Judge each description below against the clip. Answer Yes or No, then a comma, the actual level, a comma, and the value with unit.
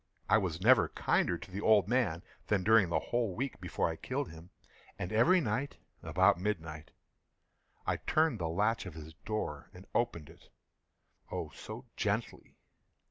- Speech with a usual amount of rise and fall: No, wide, 5.7 semitones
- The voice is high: No, low, 100 Hz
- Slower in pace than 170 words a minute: Yes, average, 155 wpm